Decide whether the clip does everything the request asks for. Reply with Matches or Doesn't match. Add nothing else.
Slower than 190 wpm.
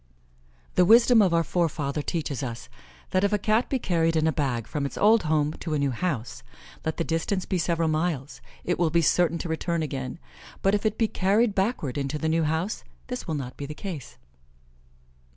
Doesn't match